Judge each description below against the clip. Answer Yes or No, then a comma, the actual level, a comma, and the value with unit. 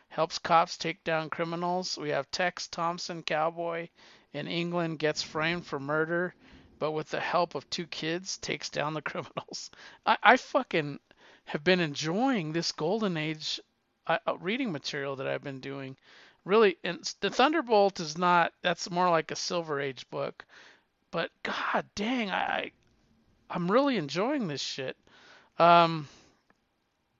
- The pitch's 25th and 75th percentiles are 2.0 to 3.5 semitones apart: Yes, average, 2.9 semitones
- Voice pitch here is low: No, medium, 170 Hz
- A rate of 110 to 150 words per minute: Yes, average, 145 wpm